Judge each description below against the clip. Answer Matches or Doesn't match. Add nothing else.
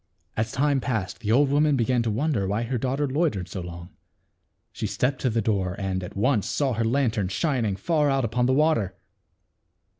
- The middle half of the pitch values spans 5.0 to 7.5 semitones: Matches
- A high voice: Doesn't match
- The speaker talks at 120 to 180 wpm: Doesn't match